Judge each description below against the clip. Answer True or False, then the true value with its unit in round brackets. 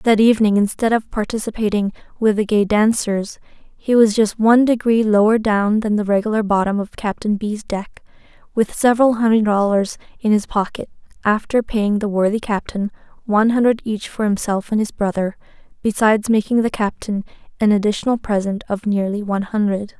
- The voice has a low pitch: False (215 Hz)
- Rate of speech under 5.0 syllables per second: False (5.4 syllables/s)